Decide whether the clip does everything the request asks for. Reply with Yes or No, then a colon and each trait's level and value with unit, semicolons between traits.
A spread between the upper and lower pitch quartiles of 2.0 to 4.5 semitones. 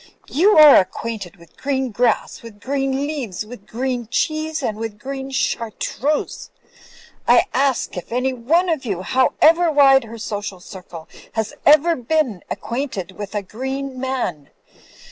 No: average, 4.9 semitones